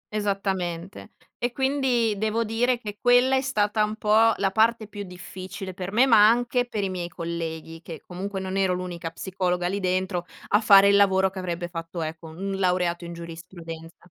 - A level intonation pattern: No, average, 3.5 semitones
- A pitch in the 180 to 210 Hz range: Yes, high, 190 Hz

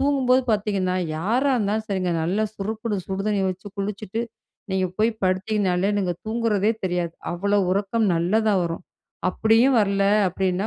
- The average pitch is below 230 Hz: Yes, high, 200 Hz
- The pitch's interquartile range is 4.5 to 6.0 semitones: No, average, 2.8 semitones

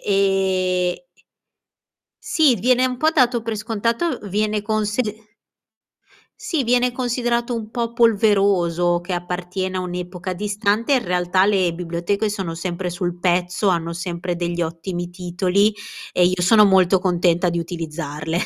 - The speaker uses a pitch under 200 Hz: Yes, high, 190 Hz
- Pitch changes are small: No, average, 3.6 semitones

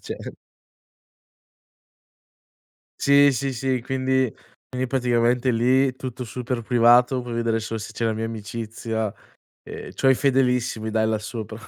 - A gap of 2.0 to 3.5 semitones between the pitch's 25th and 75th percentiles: Yes, narrow, 2.5 semitones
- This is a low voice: Yes, low, 120 Hz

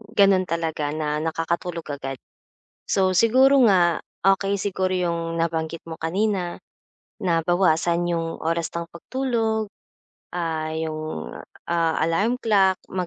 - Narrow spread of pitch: No, average, 3.1 semitones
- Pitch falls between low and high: Yes, medium, 170 Hz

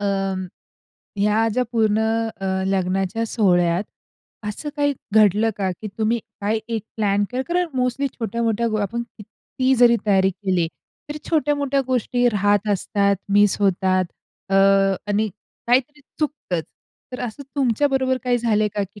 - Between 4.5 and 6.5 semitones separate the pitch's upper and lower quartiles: No, average, 4.0 semitones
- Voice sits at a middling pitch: No, high, 215 Hz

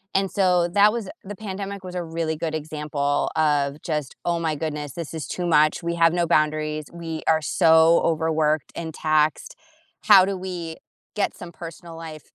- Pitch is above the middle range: No, medium, 165 Hz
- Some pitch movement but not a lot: No, narrow, 2.3 semitones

